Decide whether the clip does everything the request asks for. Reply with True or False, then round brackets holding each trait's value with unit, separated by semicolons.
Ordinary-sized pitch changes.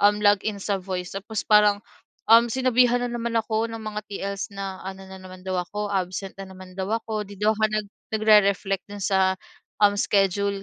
False (2.0 semitones)